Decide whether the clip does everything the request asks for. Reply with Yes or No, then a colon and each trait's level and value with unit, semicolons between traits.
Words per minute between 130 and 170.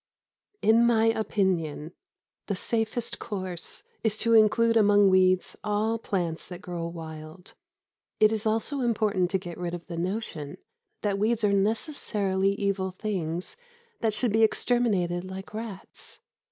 Yes: average, 140 wpm